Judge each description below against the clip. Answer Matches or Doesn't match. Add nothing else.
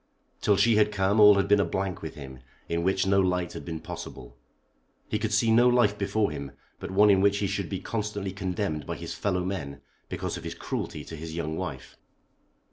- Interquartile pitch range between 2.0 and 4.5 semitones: Matches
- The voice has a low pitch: Matches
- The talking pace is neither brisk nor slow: Doesn't match